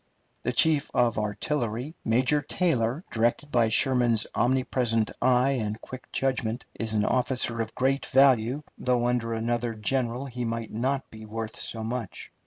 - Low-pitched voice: Yes, low, 120 Hz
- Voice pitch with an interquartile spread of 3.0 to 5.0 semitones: No, narrow, 2.6 semitones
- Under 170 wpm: Yes, average, 150 wpm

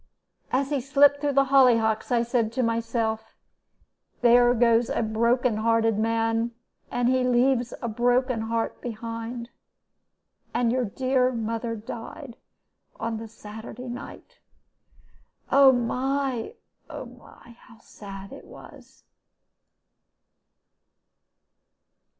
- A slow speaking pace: Yes, slow, 110 wpm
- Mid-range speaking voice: No, high, 235 Hz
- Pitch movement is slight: Yes, narrow, 1.9 semitones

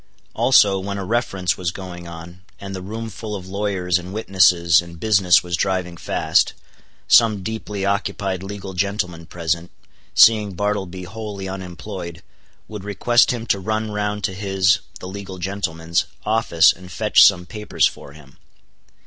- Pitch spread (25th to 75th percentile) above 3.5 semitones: No, narrow, 2.6 semitones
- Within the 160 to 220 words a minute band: No, average, 150 wpm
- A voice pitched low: Yes, very low, 95 Hz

